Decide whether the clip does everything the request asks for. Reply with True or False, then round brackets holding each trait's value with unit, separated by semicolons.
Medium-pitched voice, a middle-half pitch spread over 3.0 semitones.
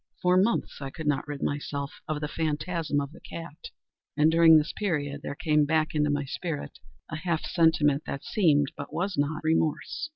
False (155 Hz; 2.5 semitones)